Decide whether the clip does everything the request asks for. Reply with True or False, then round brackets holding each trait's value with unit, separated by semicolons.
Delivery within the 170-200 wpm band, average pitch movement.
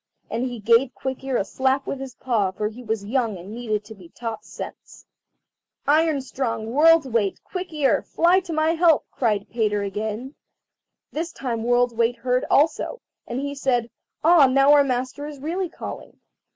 True (180 wpm; 4.3 semitones)